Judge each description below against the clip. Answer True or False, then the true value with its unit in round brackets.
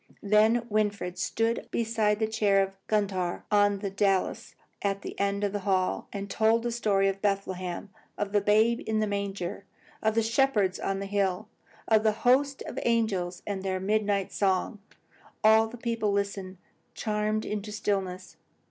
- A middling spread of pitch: False (2.0 semitones)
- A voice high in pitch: True (205 Hz)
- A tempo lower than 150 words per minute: False (165 wpm)